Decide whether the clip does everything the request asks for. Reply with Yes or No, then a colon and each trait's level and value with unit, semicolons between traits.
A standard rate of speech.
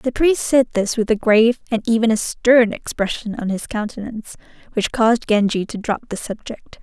Yes: average, 195 wpm